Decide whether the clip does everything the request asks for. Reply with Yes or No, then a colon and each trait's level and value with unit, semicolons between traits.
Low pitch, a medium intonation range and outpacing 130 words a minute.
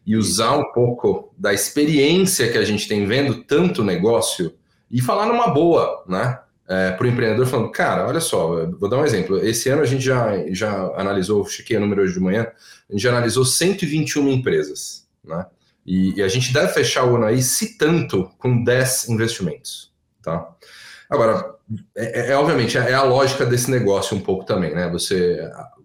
Yes: low, 120 Hz; average, 4.8 semitones; fast, 185 wpm